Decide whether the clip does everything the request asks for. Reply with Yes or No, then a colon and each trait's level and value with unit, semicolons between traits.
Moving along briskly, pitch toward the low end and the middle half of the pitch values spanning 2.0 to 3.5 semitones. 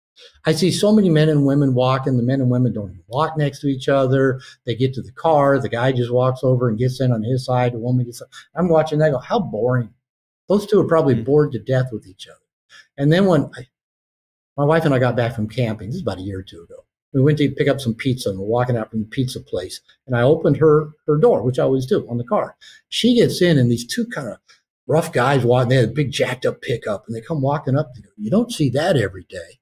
No: fast, 270 wpm; low, 130 Hz; average, 4.2 semitones